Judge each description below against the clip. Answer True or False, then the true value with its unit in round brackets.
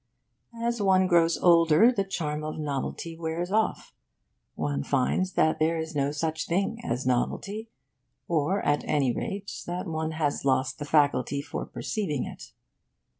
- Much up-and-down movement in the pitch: False (4.4 semitones)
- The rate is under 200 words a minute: True (150 wpm)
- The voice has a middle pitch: True (160 Hz)